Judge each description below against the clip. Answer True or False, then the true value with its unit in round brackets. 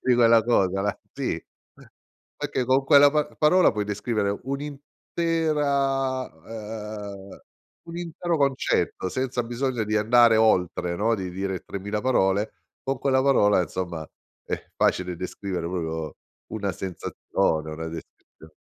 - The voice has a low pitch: True (110 Hz)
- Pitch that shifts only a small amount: False (6.0 semitones)